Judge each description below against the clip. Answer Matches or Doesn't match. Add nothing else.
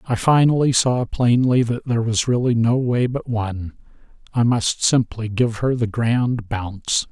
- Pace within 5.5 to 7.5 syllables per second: Doesn't match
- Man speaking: Matches